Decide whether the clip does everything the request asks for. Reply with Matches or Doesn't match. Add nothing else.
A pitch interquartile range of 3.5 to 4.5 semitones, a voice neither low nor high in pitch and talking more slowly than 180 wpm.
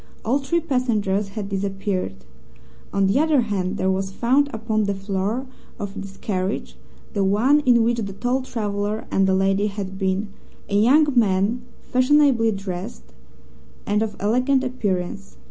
Doesn't match